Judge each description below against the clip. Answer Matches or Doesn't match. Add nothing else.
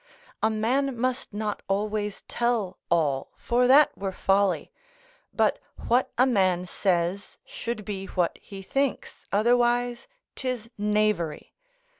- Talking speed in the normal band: Doesn't match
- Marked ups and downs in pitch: Doesn't match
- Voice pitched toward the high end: Matches